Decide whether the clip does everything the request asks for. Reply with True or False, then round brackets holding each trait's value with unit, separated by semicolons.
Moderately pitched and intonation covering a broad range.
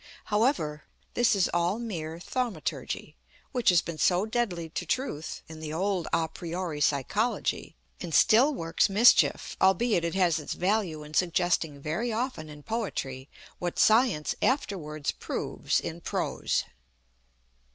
True (175 Hz; 5.7 semitones)